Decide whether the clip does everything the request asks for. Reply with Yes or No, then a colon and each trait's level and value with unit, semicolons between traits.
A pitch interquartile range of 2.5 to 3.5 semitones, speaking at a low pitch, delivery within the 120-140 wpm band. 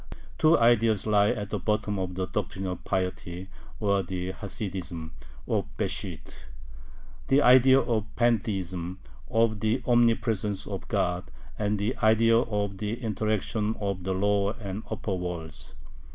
Yes: average, 3.2 semitones; low, 105 Hz; slow, 135 wpm